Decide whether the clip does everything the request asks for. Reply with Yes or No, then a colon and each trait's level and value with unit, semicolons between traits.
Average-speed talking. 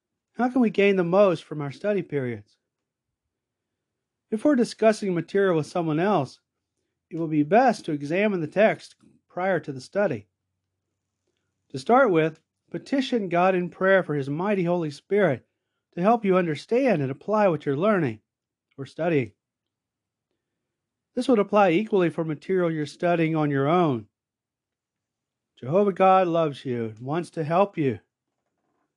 Yes: average, 150 wpm